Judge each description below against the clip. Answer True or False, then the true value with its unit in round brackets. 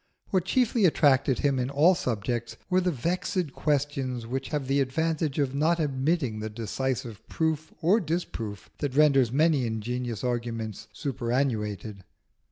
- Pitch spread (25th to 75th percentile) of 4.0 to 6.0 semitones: True (4.9 semitones)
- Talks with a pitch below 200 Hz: True (135 Hz)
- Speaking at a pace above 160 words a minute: False (140 wpm)